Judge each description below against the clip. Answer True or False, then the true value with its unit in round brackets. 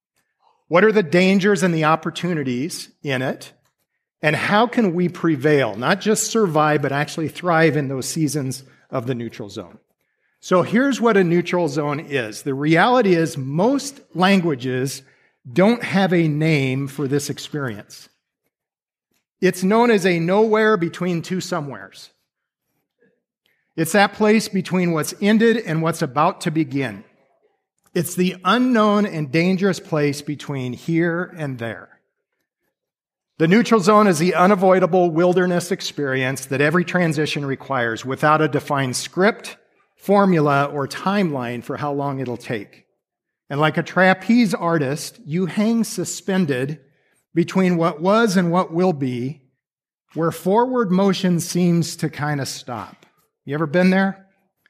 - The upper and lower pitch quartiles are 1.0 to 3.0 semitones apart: False (4.9 semitones)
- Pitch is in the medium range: True (170 Hz)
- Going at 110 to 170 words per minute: True (140 wpm)